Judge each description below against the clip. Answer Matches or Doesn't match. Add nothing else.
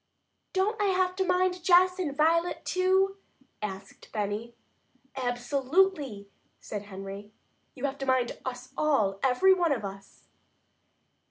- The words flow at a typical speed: Doesn't match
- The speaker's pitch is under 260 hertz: Doesn't match